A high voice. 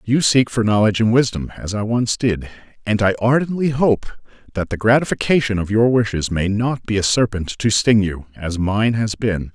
No: low, 110 Hz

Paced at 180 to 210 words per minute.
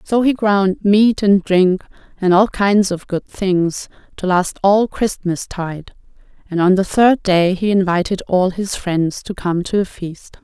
Yes: average, 185 wpm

